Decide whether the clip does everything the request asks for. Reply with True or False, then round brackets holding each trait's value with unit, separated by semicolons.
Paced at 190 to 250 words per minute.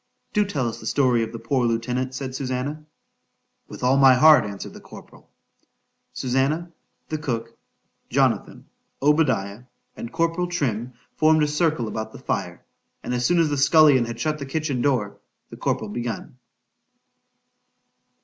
False (145 wpm)